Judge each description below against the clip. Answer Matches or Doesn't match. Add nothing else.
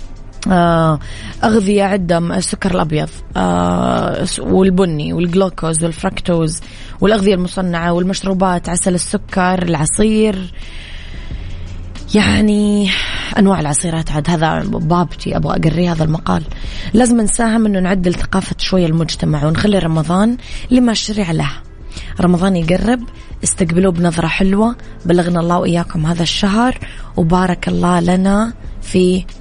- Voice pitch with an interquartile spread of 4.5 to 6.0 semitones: Doesn't match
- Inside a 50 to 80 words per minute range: Doesn't match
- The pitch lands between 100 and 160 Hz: Doesn't match